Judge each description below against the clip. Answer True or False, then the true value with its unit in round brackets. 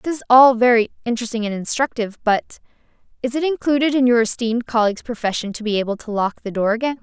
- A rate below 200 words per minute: False (205 wpm)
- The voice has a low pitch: False (235 Hz)